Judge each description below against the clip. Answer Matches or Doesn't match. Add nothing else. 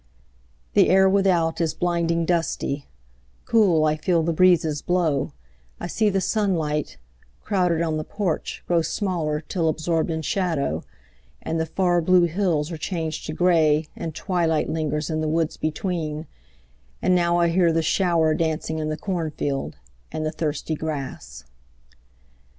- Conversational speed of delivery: Matches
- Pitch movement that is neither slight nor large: Doesn't match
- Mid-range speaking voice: Matches